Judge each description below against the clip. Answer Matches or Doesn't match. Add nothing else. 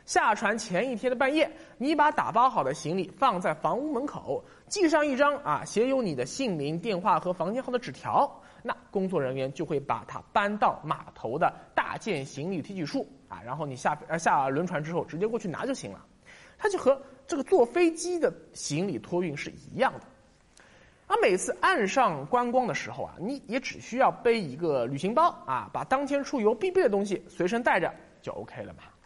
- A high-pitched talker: Matches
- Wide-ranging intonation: Matches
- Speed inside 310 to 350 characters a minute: Doesn't match